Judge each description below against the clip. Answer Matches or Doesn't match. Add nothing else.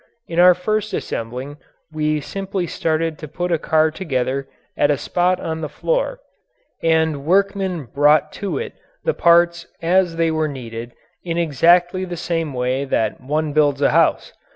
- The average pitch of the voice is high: Doesn't match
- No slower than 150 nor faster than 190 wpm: Matches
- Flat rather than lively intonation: Doesn't match